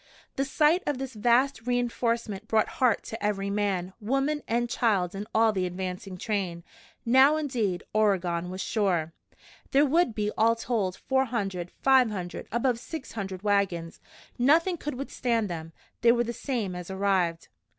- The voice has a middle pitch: No, high, 220 Hz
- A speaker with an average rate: Yes, average, 160 wpm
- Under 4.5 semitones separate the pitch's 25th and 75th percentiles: No, average, 4.9 semitones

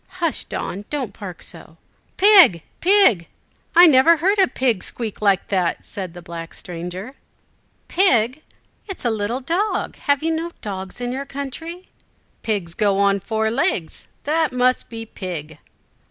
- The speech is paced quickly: No, average, 155 wpm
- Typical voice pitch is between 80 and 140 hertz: No, high, 235 Hz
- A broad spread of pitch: Yes, wide, 8.8 semitones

